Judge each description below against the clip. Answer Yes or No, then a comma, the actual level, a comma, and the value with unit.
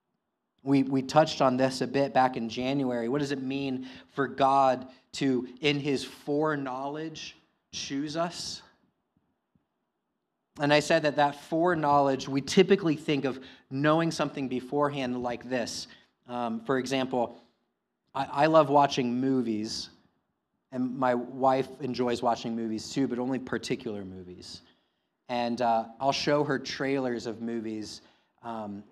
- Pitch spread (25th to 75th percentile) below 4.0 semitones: Yes, average, 2.9 semitones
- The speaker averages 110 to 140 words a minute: Yes, slow, 135 wpm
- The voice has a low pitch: Yes, low, 130 Hz